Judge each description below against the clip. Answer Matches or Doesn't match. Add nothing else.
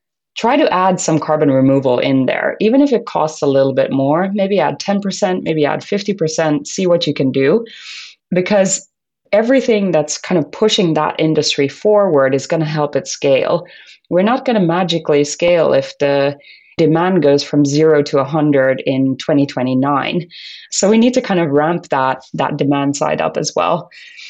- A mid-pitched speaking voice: Matches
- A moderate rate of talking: Matches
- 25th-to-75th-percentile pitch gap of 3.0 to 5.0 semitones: Doesn't match